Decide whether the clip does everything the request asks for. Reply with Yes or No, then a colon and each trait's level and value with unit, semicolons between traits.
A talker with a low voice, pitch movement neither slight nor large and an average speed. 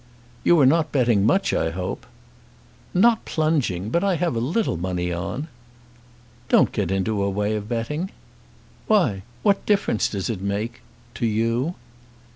No: low, 115 Hz; wide, 8.6 semitones; average, 150 wpm